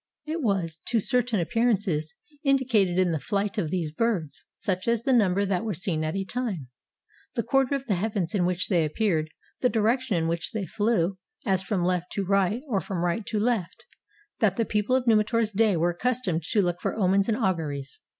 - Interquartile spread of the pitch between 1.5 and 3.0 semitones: No, average, 4.5 semitones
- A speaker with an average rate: No, fast, 220 wpm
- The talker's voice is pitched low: No, high, 200 Hz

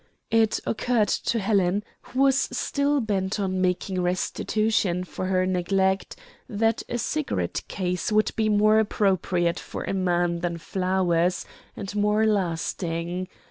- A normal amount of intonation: Yes, average, 3.0 semitones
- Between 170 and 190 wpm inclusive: No, slow, 135 wpm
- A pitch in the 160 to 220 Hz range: Yes, high, 190 Hz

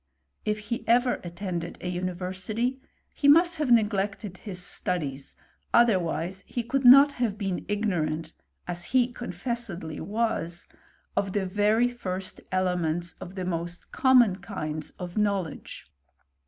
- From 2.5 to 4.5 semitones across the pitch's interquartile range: No, average, 5.0 semitones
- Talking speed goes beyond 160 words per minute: No, slow, 135 wpm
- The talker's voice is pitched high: Yes, high, 195 Hz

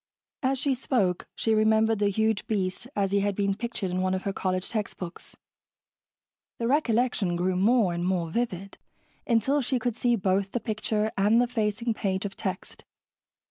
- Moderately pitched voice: No, high, 210 Hz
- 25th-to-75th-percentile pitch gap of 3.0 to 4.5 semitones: Yes, average, 3.7 semitones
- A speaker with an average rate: Yes, average, 175 wpm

